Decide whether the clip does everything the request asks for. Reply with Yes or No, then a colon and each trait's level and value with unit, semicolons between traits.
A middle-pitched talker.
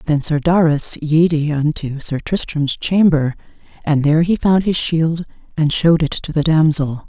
Yes: medium, 155 Hz